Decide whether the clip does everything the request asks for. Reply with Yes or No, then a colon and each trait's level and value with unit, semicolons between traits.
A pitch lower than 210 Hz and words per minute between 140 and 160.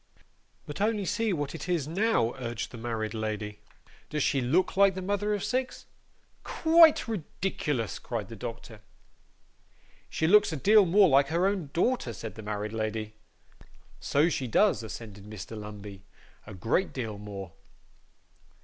Yes: low, 135 Hz; average, 150 wpm